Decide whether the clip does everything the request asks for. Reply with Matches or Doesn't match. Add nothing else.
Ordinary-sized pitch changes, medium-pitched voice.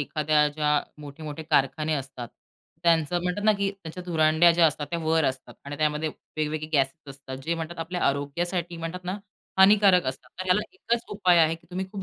Matches